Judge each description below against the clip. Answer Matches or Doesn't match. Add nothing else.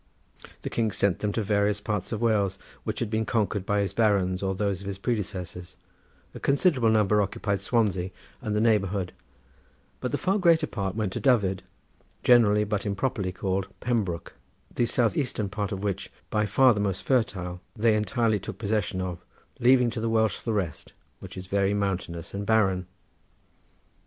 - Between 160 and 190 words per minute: Matches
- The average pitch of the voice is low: Matches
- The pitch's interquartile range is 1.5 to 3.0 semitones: Matches